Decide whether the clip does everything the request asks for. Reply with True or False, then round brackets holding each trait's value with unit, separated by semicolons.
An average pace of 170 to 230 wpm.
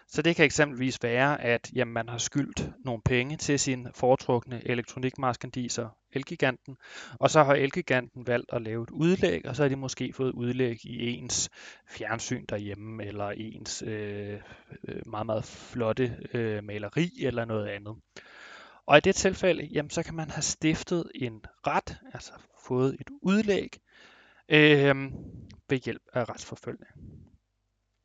False (150 wpm)